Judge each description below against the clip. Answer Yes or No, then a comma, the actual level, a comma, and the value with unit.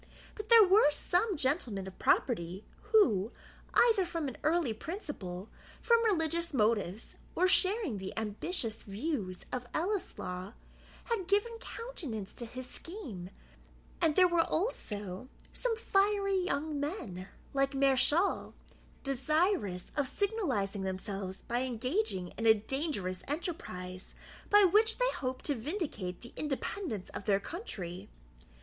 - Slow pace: Yes, slow, 125 wpm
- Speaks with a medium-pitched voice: No, very high, 275 Hz